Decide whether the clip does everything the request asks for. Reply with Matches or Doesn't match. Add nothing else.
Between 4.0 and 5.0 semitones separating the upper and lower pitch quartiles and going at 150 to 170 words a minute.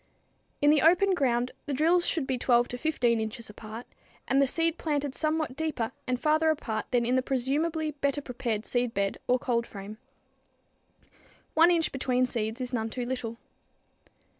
Matches